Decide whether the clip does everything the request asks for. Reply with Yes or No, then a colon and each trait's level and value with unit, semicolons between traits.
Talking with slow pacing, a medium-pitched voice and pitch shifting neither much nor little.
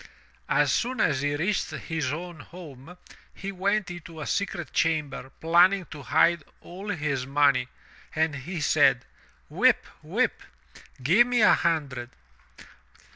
Yes: slow, 130 wpm; medium, 160 Hz; average, 4.1 semitones